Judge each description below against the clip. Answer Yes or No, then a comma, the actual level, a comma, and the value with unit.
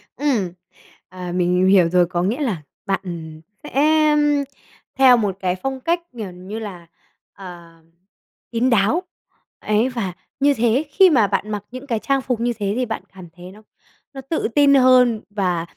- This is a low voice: No, high, 220 Hz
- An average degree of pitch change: No, wide, 6.0 semitones